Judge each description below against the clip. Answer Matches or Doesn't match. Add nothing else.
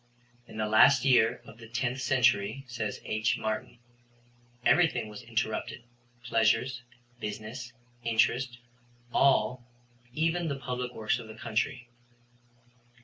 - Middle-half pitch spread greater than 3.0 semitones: Doesn't match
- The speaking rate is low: Matches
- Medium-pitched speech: Doesn't match